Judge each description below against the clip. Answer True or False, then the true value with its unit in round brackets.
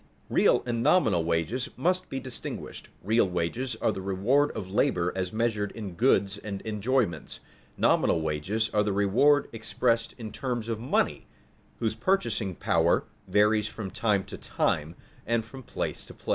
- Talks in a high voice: False (110 Hz)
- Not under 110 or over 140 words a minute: False (160 wpm)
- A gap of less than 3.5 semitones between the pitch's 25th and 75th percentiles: False (3.8 semitones)